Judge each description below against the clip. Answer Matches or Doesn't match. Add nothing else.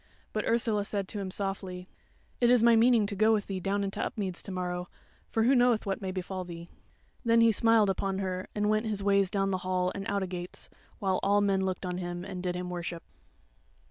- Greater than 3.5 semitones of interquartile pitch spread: Doesn't match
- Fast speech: Matches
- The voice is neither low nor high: Doesn't match